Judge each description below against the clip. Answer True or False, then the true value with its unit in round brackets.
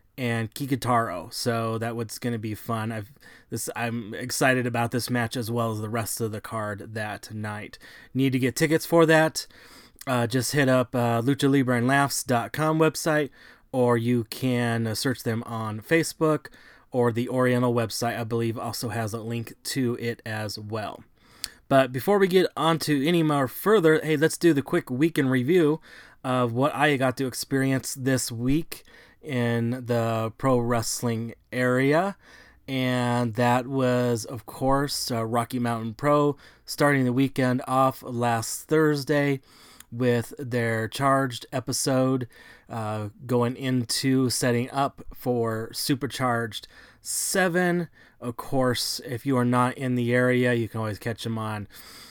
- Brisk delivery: False (155 wpm)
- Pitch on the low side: True (125 Hz)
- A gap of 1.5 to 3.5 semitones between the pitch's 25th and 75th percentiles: True (2.9 semitones)